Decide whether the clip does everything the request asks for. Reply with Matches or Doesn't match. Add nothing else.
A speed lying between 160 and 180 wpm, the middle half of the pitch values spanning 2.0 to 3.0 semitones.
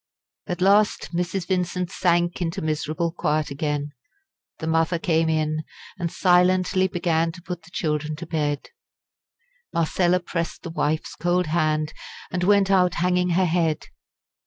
Doesn't match